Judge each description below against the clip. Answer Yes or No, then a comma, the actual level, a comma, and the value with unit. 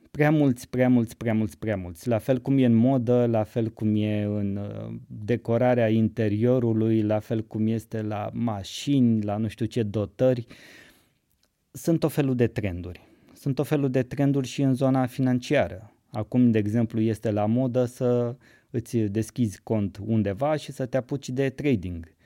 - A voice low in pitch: Yes, low, 115 Hz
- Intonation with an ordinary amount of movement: Yes, average, 3.2 semitones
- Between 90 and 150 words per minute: No, fast, 170 wpm